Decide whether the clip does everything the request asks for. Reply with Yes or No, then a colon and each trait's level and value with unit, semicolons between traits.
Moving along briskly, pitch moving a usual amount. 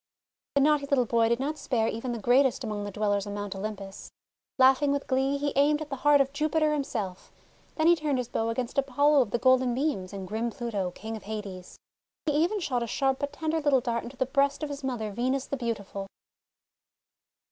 Yes: fast, 210 wpm; average, 4.5 semitones